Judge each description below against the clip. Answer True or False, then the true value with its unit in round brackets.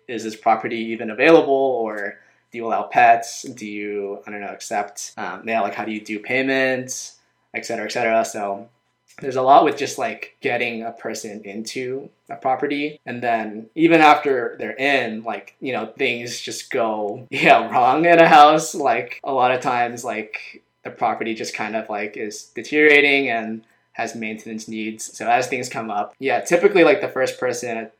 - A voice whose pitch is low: True (115 Hz)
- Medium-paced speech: True (185 wpm)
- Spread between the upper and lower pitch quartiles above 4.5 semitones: False (3.3 semitones)